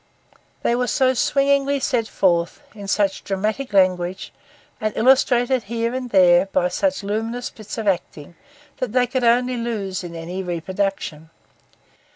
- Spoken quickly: No, average, 145 wpm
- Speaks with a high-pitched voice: Yes, high, 215 Hz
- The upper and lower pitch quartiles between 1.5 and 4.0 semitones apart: No, average, 4.8 semitones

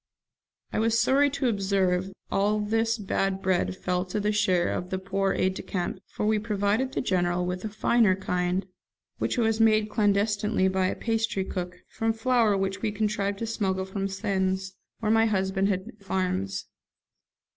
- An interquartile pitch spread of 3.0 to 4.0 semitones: No, narrow, 2.5 semitones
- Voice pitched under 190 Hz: No, high, 195 Hz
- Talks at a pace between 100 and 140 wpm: No, average, 175 wpm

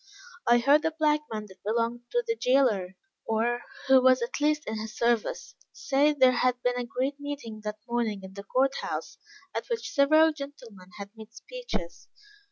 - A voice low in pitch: No, high, 245 Hz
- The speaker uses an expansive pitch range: No, average, 4.7 semitones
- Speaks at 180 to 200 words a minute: Yes, average, 185 wpm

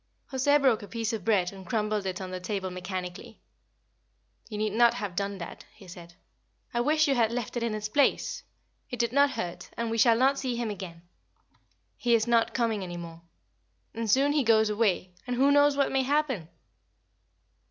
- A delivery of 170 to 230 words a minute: Yes, average, 195 wpm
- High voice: Yes, high, 225 Hz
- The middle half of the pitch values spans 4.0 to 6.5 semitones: Yes, average, 4.7 semitones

